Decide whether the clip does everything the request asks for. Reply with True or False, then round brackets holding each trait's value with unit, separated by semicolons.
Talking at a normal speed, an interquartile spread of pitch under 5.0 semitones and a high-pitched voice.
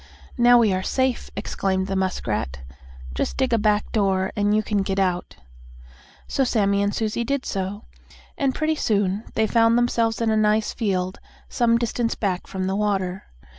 True (170 wpm; 3.3 semitones; 210 Hz)